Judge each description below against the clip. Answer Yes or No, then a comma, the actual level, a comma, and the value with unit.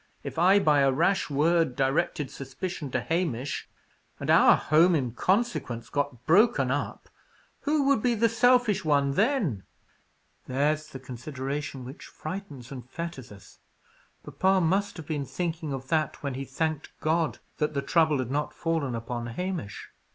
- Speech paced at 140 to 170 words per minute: Yes, average, 155 wpm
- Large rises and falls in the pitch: No, average, 5.0 semitones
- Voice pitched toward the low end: No, medium, 150 Hz